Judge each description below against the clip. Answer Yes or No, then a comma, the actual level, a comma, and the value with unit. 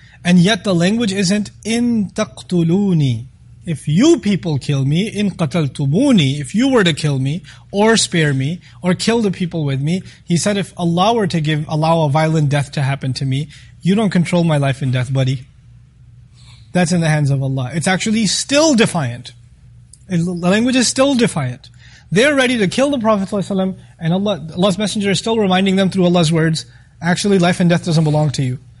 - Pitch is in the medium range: Yes, medium, 170 Hz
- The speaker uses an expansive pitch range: Yes, wide, 6.5 semitones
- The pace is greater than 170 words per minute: Yes, average, 195 wpm